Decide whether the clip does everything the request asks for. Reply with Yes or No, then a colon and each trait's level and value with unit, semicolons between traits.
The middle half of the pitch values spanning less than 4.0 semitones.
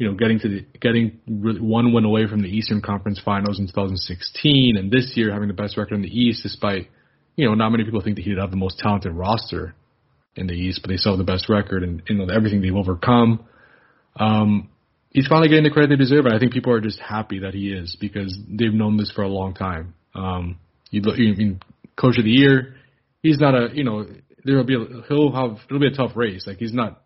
Yes: average, 3.4 semitones